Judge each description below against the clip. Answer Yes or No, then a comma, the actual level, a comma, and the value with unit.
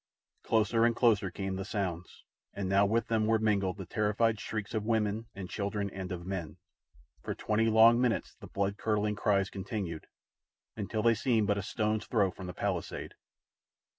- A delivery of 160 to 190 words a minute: Yes, average, 175 wpm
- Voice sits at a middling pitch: No, low, 105 Hz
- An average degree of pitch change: No, narrow, 2.3 semitones